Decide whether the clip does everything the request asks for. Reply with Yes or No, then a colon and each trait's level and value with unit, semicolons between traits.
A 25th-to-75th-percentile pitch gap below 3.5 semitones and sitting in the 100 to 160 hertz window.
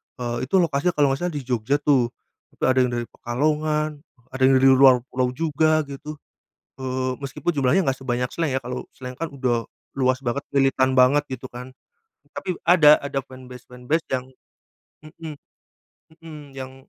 Yes: average, 2.9 semitones; low, 135 Hz